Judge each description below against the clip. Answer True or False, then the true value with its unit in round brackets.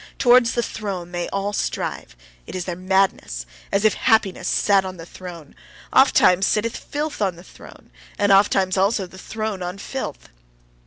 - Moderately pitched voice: False (195 Hz)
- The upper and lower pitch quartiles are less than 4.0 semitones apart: True (2.9 semitones)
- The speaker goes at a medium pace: True (165 wpm)